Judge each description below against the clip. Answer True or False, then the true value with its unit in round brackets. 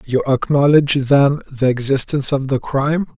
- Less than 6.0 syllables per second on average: True (5.3 syllables/s)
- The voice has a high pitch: False (135 Hz)